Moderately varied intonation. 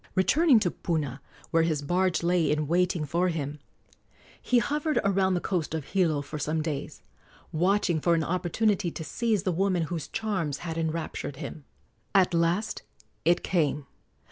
Yes: average, 3.3 semitones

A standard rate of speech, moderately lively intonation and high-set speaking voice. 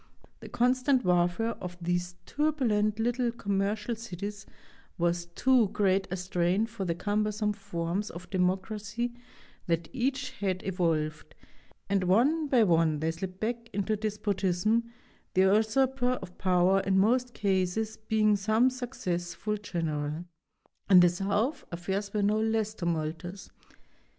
No: slow, 130 wpm; average, 4.0 semitones; high, 200 Hz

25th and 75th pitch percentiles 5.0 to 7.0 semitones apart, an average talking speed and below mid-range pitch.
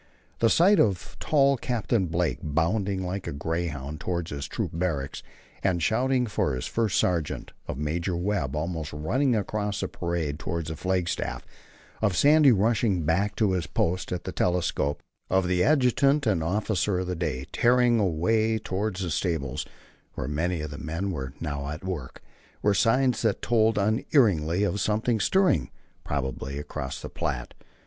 Yes: wide, 5.6 semitones; average, 160 wpm; very low, 90 Hz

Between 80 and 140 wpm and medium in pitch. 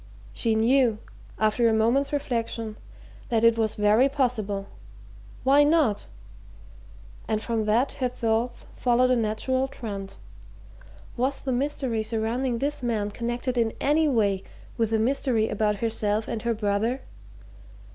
No: slow, 135 wpm; high, 230 Hz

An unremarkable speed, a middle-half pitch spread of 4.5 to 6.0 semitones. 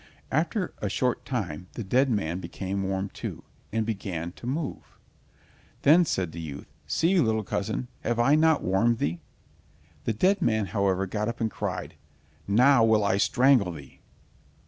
Yes: average, 160 wpm; average, 5.3 semitones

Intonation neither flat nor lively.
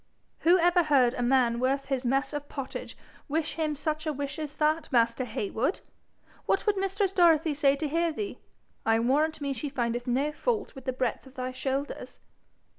Yes: average, 3.7 semitones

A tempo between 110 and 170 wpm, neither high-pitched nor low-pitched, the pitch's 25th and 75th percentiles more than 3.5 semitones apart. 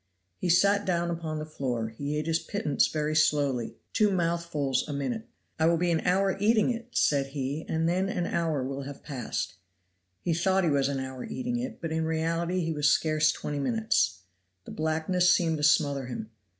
No: average, 195 wpm; medium, 160 Hz; average, 3.9 semitones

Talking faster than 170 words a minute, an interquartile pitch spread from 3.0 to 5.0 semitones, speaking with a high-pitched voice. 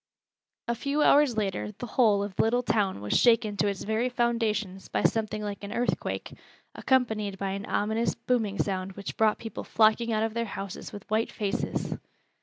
No: average, 185 wpm; narrow, 2.6 semitones; high, 215 Hz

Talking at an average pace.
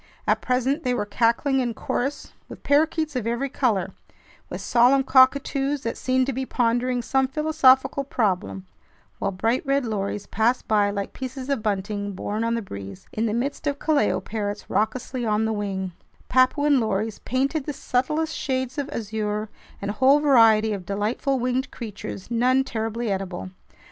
Yes: average, 165 wpm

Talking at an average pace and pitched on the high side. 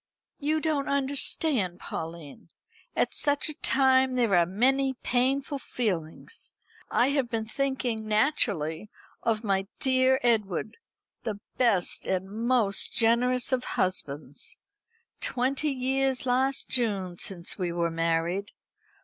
No: slow, 115 wpm; high, 235 Hz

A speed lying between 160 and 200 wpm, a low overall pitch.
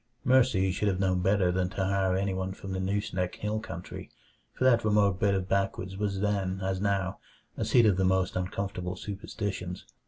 Yes: average, 185 wpm; very low, 95 Hz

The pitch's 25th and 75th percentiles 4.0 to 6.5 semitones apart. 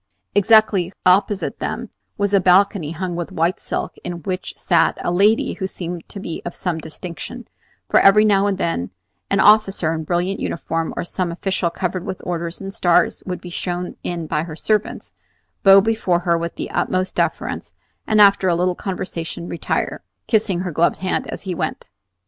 No: narrow, 2.4 semitones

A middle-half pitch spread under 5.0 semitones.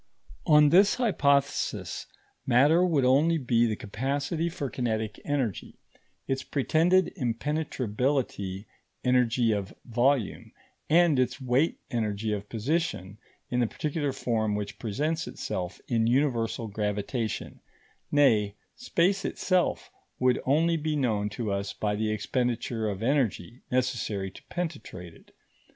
No: wide, 5.4 semitones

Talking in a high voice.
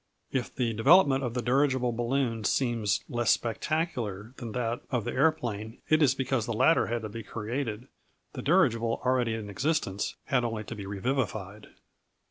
No: low, 120 Hz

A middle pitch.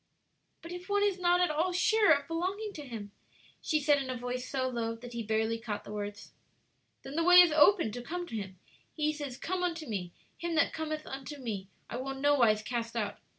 No: very high, 280 Hz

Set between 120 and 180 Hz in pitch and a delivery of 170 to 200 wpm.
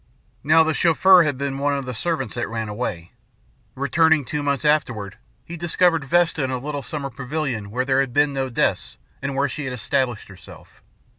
Yes: medium, 140 Hz; average, 195 wpm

